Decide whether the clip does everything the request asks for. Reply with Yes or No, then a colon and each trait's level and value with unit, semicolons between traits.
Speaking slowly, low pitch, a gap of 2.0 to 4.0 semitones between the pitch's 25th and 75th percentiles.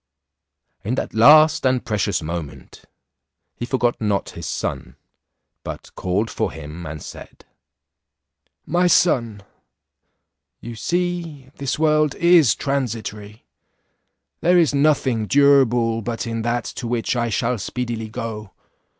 No: slow, 120 wpm; low, 120 Hz; average, 4.7 semitones